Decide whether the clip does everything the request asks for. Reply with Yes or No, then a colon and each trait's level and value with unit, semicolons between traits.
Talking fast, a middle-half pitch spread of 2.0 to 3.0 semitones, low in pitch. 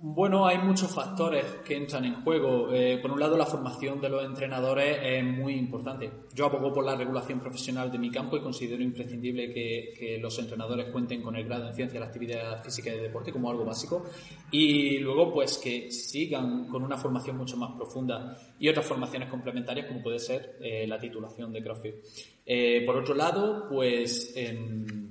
Yes: fast, 195 wpm; narrow, 2.6 semitones; low, 125 Hz